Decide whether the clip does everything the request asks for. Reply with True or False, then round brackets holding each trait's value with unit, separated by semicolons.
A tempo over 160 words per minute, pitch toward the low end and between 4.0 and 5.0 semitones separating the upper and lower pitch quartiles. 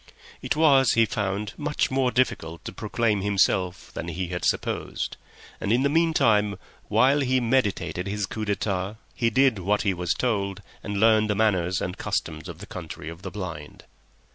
True (175 wpm; 105 Hz; 4.3 semitones)